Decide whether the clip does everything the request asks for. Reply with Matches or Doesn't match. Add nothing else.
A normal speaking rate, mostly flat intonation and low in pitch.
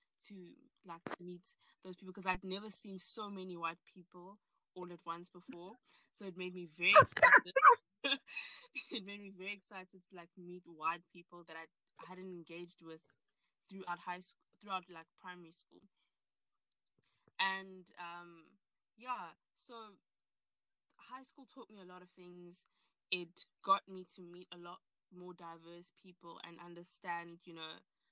Doesn't match